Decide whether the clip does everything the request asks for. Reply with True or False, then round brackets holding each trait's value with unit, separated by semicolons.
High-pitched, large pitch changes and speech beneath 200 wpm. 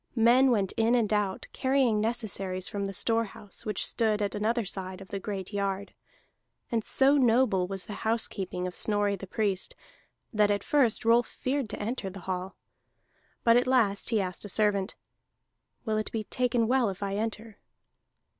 False (210 Hz; 2.9 semitones; 175 wpm)